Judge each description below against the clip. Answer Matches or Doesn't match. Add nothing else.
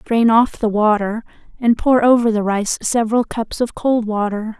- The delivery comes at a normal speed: Matches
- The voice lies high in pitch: Matches